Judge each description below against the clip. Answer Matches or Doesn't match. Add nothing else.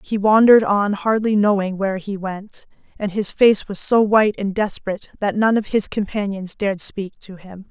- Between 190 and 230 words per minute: Matches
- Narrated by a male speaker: Doesn't match